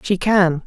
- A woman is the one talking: Yes, female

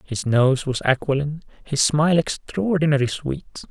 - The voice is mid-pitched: Yes, medium, 145 Hz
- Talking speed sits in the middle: No, slow, 130 wpm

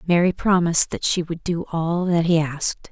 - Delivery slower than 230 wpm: Yes, fast, 205 wpm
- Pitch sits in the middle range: Yes, medium, 170 Hz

